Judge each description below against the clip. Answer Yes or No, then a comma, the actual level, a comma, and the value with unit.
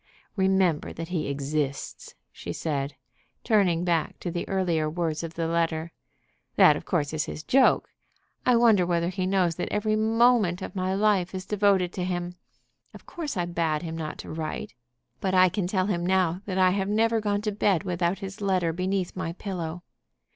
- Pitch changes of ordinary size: Yes, average, 3.0 semitones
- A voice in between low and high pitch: Yes, medium, 180 Hz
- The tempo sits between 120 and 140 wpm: No, average, 185 wpm